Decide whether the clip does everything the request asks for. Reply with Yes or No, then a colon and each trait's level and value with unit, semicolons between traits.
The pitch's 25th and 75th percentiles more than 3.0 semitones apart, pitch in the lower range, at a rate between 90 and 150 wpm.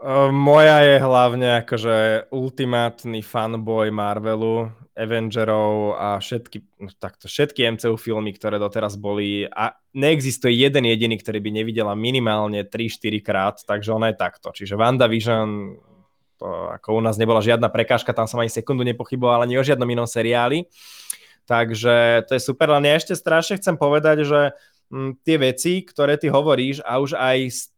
No: average, 3.4 semitones; low, 120 Hz; average, 160 wpm